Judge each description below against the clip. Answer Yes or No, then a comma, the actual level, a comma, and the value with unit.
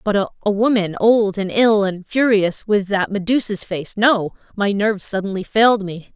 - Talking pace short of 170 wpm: Yes, average, 145 wpm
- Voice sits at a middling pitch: No, high, 205 Hz